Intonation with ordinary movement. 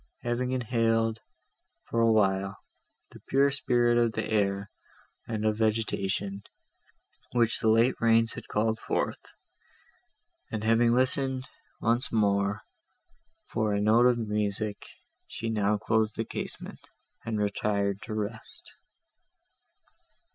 No: narrow, 1.9 semitones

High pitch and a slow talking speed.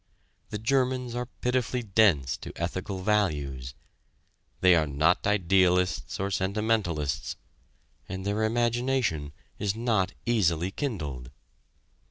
No: very low, 95 Hz; slow, 105 wpm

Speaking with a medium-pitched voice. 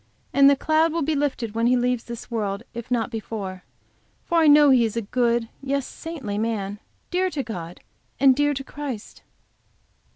No: very high, 250 Hz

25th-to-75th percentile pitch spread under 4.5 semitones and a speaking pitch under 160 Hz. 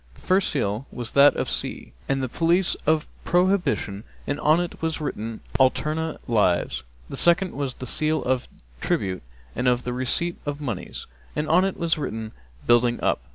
No: average, 5.3 semitones; medium, 140 Hz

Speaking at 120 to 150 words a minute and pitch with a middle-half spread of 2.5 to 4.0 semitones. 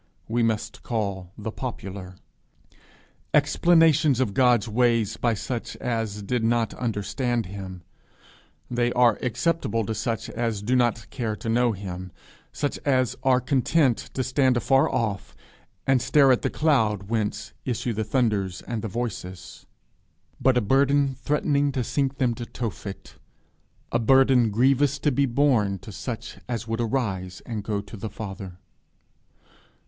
Yes: average, 145 wpm; average, 3.7 semitones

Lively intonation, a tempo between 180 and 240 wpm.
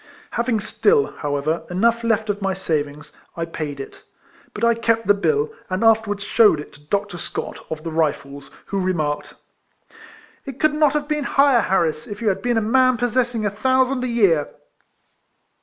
Yes: wide, 6.8 semitones; average, 185 wpm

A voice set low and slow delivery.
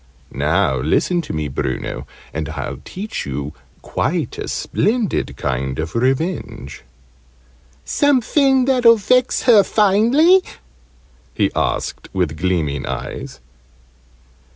No: medium, 165 Hz; slow, 105 wpm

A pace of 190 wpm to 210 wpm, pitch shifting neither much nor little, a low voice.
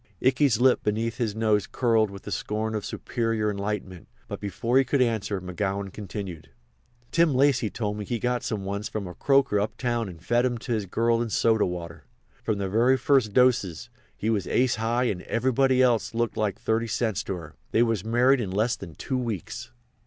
Yes: average, 195 wpm; average, 3.2 semitones; low, 110 Hz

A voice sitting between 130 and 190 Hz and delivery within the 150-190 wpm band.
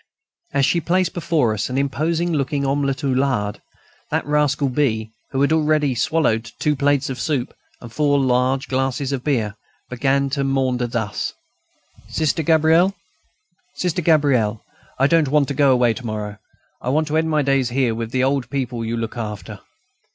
Yes: low, 135 Hz; average, 175 wpm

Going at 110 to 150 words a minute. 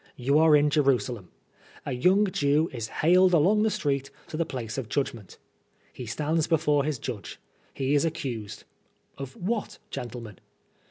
No: average, 160 wpm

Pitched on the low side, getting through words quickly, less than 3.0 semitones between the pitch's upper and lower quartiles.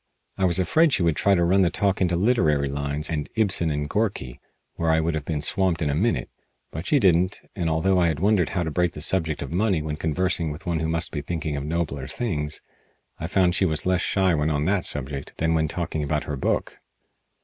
No: very low, 80 Hz; fast, 235 wpm; average, 3.6 semitones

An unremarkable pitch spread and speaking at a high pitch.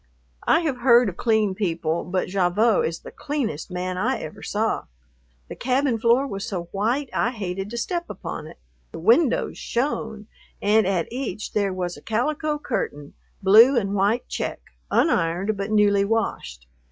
Yes: average, 4.6 semitones; high, 215 Hz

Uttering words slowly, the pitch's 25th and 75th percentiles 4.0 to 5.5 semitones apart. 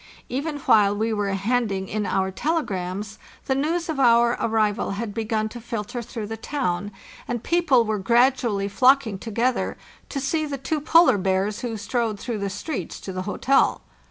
No: average, 170 wpm; average, 4.5 semitones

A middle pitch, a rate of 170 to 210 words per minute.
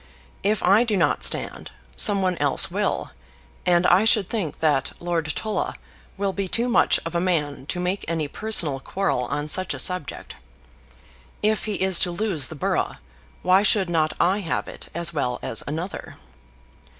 Yes: medium, 180 Hz; average, 175 wpm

